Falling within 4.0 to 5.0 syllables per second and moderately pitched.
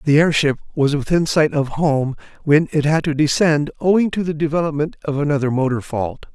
No: 5.4 syllables/s; medium, 150 Hz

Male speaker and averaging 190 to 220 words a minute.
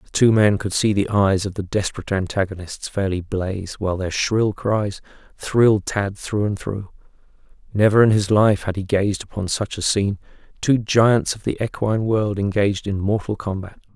No: male; average, 180 wpm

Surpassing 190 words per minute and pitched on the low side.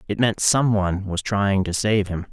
Yes: fast, 205 wpm; low, 100 Hz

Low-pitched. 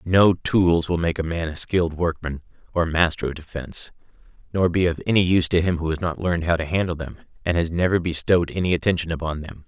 Yes: very low, 85 Hz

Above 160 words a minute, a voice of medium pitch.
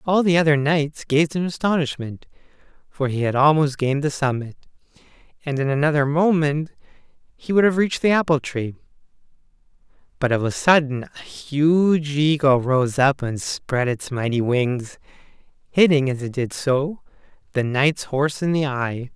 No: average, 155 wpm; medium, 145 Hz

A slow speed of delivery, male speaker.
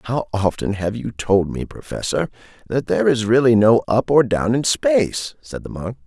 No: average, 200 wpm; male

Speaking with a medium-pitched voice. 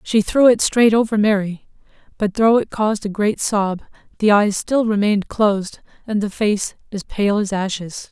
No: high, 210 Hz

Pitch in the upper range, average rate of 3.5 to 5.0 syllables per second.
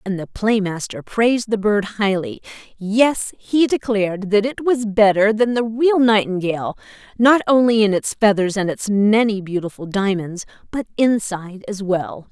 Yes: high, 210 Hz; 4.6 syllables/s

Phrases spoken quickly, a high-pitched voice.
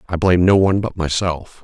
No: fast, 220 wpm; very low, 90 Hz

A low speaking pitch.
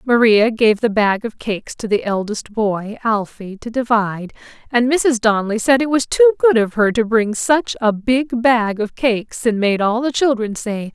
No: high, 230 Hz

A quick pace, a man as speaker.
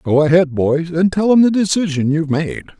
Yes: fast, 215 wpm; male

